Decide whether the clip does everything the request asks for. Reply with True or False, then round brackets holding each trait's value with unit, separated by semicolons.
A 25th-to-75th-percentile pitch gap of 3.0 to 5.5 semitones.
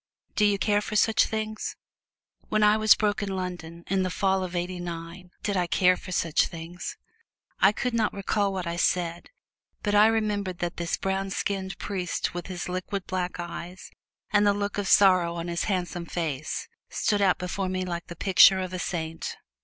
False (2.6 semitones)